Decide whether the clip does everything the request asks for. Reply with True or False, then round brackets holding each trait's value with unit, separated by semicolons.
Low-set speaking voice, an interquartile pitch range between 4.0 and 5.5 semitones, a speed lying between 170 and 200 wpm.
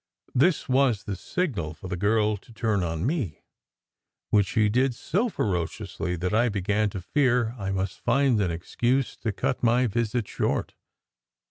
False (110 Hz; 4.6 semitones; 160 wpm)